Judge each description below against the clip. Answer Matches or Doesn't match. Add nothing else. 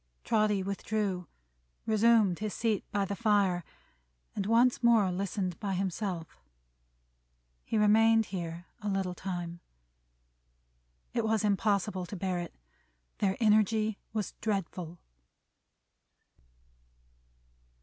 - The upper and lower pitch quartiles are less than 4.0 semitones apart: Matches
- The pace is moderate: Doesn't match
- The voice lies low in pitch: Doesn't match